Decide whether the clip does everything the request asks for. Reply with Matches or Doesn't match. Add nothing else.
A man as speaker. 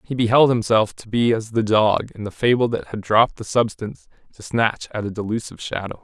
Matches